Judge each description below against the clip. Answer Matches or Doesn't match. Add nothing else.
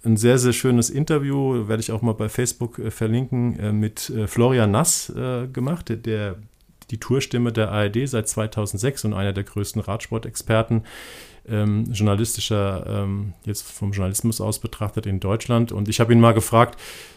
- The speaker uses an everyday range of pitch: Doesn't match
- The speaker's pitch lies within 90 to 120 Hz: Matches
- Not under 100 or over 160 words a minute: Matches